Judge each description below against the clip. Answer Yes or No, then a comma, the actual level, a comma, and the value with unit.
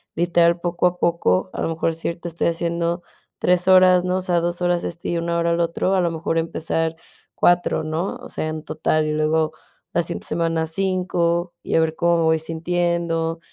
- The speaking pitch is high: No, medium, 170 Hz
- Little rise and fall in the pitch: Yes, narrow, 1.1 semitones